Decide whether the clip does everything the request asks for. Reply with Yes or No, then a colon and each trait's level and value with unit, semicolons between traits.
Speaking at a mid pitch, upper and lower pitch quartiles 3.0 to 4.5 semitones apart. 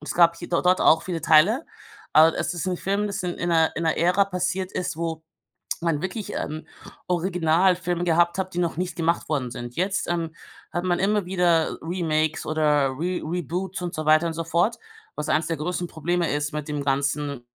No: medium, 170 Hz; narrow, 2.5 semitones